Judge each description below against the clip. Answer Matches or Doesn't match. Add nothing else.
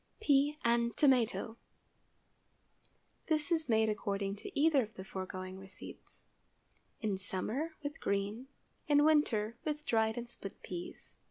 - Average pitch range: Doesn't match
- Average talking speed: Doesn't match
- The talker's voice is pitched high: Matches